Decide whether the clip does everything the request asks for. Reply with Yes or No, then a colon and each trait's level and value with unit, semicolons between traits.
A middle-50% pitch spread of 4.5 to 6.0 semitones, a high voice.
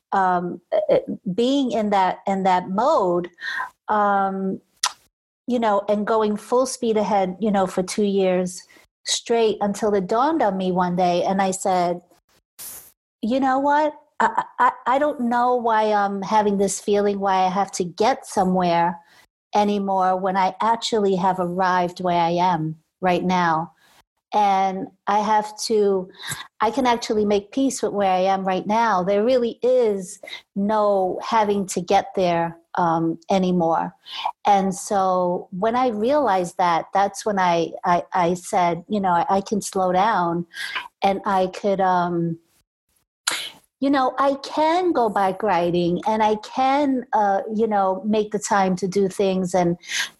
No: average, 3.3 semitones; high, 200 Hz